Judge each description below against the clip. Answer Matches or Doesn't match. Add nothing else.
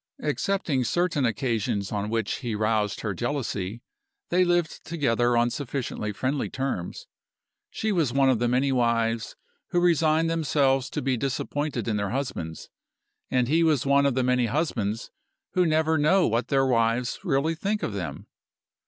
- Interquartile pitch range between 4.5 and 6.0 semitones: Matches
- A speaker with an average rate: Matches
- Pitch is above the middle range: Doesn't match